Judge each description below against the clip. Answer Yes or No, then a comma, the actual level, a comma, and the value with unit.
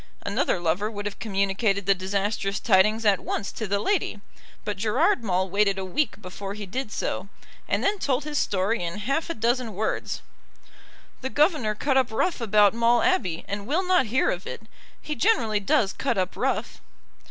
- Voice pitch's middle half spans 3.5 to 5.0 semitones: Yes, average, 4.7 semitones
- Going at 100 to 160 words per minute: No, average, 185 wpm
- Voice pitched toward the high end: Yes, high, 210 Hz